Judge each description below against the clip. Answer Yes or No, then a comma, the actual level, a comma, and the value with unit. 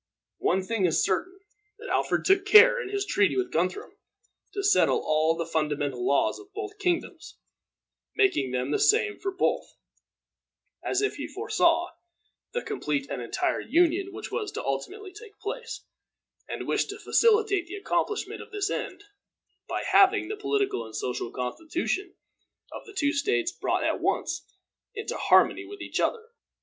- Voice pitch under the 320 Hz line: No, very high, 385 Hz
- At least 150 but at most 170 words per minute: Yes, average, 160 wpm